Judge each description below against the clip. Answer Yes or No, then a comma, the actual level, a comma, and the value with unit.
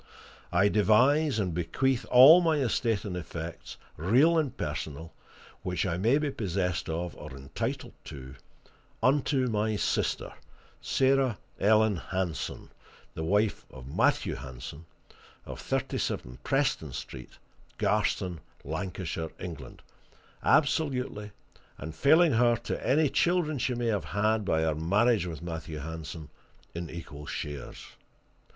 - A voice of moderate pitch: No, low, 100 Hz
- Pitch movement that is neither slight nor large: No, wide, 7.8 semitones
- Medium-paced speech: No, slow, 125 wpm